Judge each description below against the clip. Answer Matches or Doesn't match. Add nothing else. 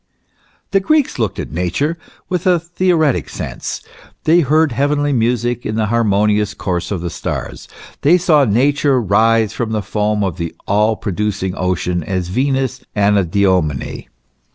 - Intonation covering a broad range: Matches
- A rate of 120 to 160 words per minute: Matches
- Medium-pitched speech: Doesn't match